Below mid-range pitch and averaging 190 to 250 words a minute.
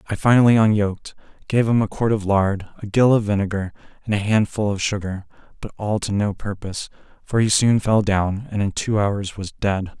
Yes: low, 105 Hz; fast, 205 wpm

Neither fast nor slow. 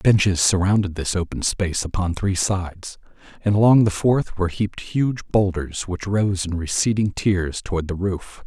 Yes: average, 170 wpm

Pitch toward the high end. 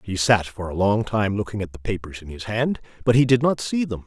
No: low, 110 Hz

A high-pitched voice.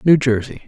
No: low, 130 Hz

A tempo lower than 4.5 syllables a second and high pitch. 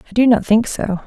No: 5.2 syllables/s; high, 220 Hz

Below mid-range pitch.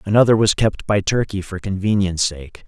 Yes: low, 100 Hz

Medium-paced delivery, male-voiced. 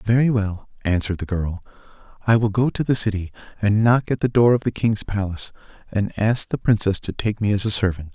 No: fast, 220 wpm; male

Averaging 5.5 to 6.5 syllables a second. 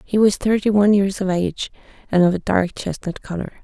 Yes: 5.9 syllables/s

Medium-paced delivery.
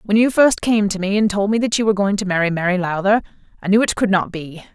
No: fast, 290 wpm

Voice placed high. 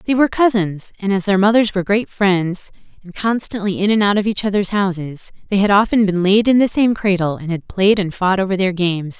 Yes: high, 195 Hz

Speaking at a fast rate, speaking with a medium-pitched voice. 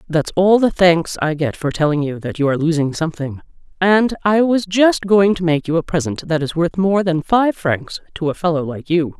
Yes: fast, 235 wpm; medium, 170 Hz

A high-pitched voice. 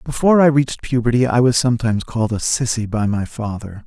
No: low, 120 Hz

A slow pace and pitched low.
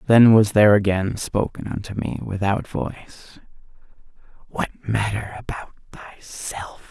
Yes: slow, 115 wpm; low, 105 Hz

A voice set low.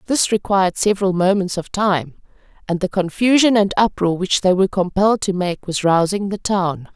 No: high, 190 Hz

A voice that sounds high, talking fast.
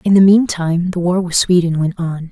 No: medium, 175 Hz; fast, 260 wpm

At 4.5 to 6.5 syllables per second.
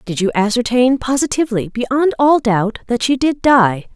Yes: 4.7 syllables/s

